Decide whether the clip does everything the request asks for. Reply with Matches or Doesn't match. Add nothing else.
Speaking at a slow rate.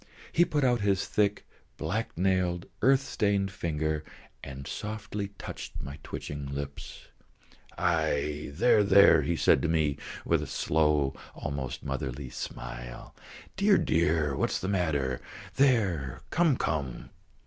Matches